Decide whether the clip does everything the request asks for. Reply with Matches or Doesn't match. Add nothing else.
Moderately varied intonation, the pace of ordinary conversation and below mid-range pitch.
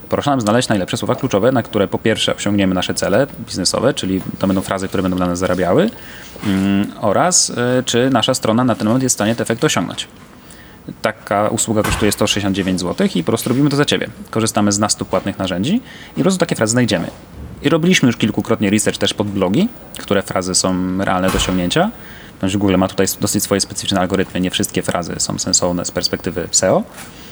Doesn't match